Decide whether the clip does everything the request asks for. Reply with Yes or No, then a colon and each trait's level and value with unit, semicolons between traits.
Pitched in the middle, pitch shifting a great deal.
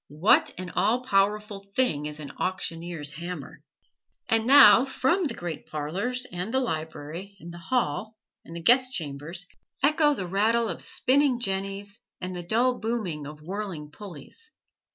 No: high, 195 Hz; wide, 6.4 semitones